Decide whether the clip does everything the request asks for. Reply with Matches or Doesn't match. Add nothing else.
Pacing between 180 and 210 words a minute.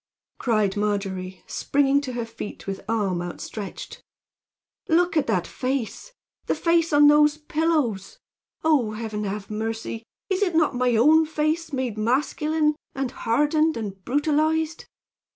Doesn't match